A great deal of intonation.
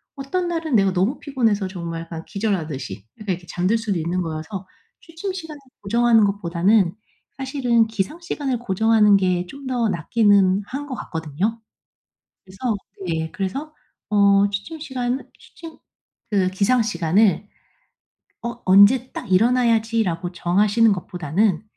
No: average, 4.8 semitones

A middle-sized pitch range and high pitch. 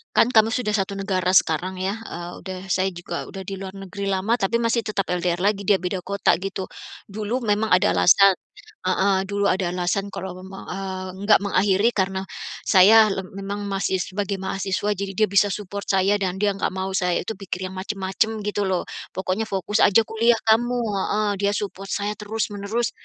No: narrow, 1.7 semitones; high, 195 Hz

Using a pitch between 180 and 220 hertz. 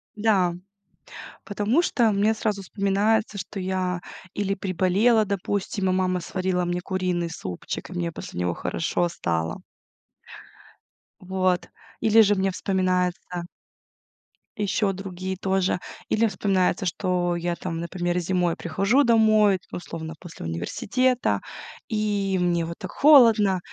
Yes: high, 190 Hz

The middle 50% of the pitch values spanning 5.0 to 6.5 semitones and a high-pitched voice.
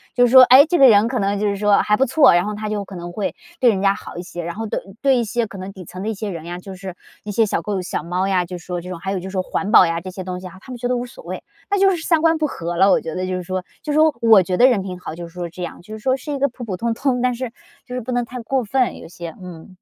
Yes: average, 5.3 semitones; high, 205 Hz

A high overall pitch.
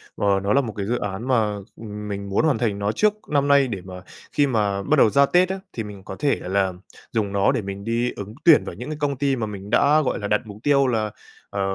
No: low, 110 Hz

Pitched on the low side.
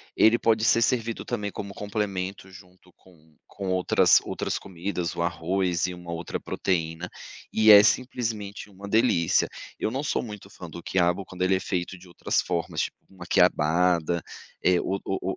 Yes: very low, 95 Hz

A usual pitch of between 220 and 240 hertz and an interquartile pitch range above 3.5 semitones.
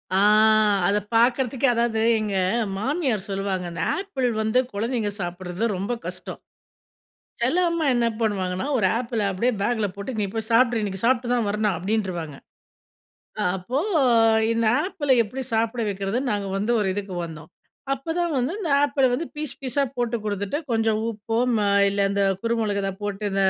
Yes: high, 225 Hz; average, 3.9 semitones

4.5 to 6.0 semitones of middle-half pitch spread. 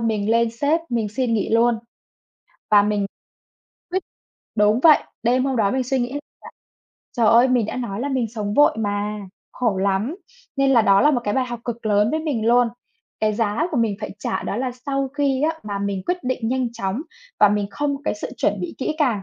No: average, 4.0 semitones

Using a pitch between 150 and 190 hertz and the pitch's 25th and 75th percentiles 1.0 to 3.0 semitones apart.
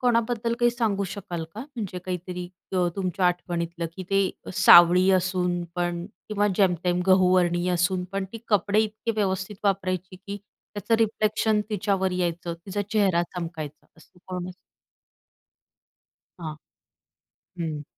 Yes: medium, 185 Hz; average, 2.7 semitones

